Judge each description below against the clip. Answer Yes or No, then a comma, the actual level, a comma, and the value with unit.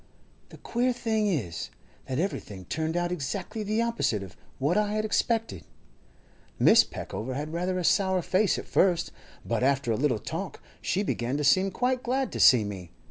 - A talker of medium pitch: Yes, medium, 175 Hz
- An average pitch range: No, wide, 8.4 semitones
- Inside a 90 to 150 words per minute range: No, average, 180 wpm